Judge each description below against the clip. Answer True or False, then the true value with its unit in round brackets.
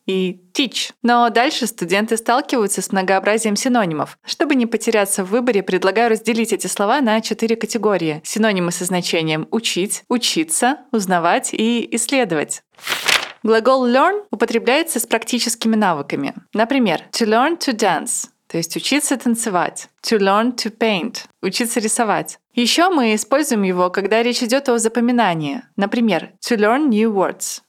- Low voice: False (225 Hz)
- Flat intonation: False (3.6 semitones)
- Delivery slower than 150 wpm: True (140 wpm)